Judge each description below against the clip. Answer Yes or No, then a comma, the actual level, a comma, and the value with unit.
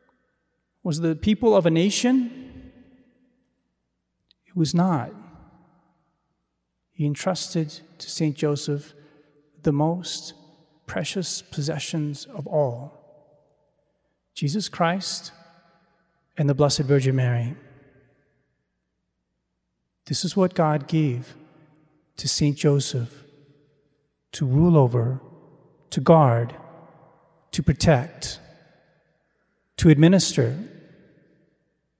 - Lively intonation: No, narrow, 2.6 semitones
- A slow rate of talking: Yes, slow, 85 wpm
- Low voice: No, medium, 155 Hz